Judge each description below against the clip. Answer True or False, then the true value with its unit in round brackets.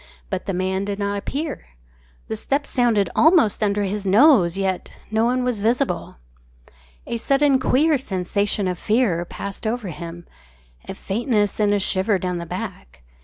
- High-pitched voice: True (205 Hz)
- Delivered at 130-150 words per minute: False (160 wpm)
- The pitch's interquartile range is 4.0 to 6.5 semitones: True (4.6 semitones)